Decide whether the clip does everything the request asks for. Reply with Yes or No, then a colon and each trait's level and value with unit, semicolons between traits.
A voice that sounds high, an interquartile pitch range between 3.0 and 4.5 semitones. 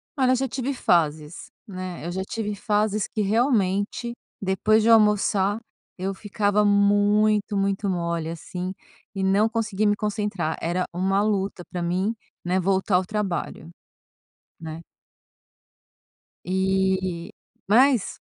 No: high, 195 Hz; narrow, 2.5 semitones